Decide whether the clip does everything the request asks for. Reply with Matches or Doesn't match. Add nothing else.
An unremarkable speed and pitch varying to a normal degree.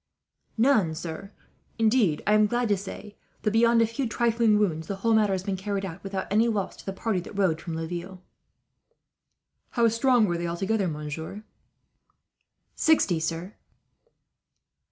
Matches